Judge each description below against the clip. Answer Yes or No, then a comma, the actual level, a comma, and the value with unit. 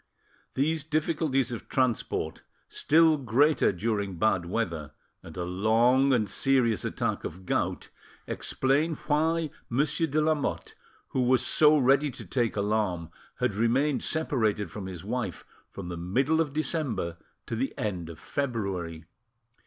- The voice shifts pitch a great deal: Yes, wide, 7.0 semitones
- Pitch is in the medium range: No, low, 120 Hz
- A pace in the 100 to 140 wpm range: Yes, slow, 135 wpm